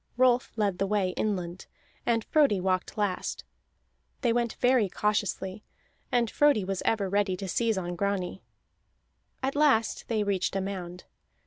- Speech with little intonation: No, average, 3.6 semitones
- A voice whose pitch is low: No, high, 205 Hz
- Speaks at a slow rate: No, average, 145 wpm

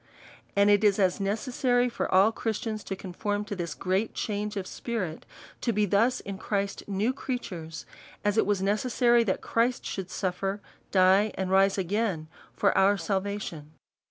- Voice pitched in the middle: No, high, 200 Hz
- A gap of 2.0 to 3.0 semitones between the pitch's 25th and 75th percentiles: Yes, narrow, 2.6 semitones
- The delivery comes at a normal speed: Yes, average, 160 wpm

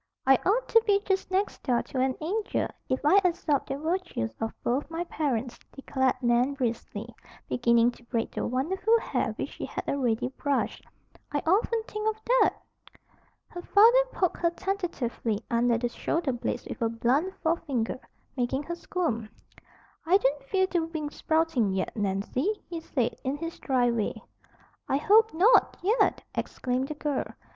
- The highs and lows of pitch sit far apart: Yes, wide, 6.9 semitones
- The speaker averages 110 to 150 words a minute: No, average, 165 wpm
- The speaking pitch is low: No, very high, 285 Hz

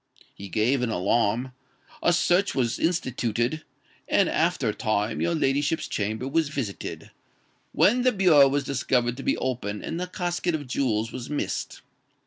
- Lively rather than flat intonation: Yes, wide, 5.8 semitones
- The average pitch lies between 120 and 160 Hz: Yes, low, 135 Hz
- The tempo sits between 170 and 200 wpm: No, average, 155 wpm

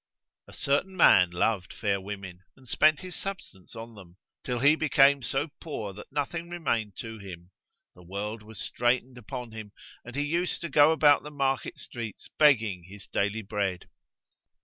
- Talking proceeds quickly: No, average, 170 wpm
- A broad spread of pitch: Yes, wide, 6.3 semitones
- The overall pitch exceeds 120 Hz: No, low, 115 Hz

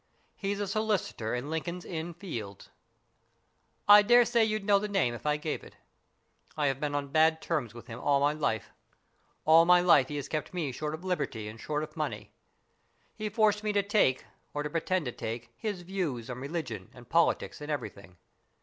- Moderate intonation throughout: No, wide, 6.7 semitones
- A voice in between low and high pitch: Yes, medium, 155 Hz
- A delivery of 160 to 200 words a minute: Yes, average, 195 wpm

